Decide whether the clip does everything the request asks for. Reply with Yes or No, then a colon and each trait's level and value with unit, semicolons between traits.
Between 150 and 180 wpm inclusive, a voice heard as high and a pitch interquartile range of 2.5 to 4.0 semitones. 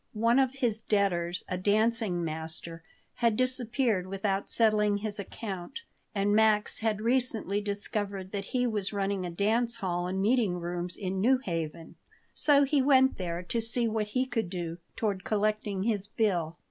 Yes: average, 160 wpm; high, 205 Hz; average, 3.7 semitones